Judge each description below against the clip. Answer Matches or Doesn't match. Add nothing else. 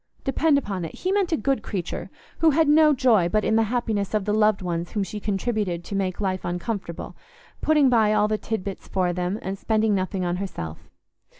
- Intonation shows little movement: Doesn't match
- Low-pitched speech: Doesn't match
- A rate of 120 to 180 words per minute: Doesn't match